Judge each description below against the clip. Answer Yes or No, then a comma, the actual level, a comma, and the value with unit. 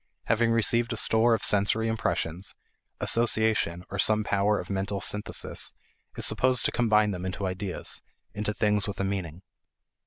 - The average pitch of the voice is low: Yes, low, 105 Hz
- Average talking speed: Yes, average, 155 wpm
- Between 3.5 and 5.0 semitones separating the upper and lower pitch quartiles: No, narrow, 2.5 semitones